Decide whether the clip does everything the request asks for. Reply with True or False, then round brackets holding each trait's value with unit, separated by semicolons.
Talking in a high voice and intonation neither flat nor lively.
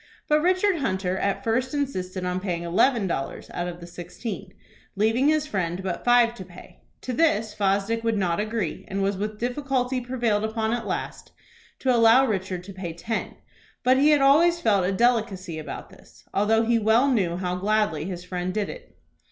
True (215 Hz; 4.9 semitones)